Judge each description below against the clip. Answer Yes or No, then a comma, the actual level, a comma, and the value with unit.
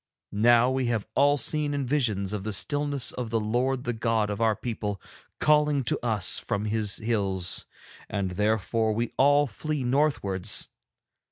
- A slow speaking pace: No, average, 155 wpm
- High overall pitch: No, low, 115 Hz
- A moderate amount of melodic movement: Yes, average, 4.5 semitones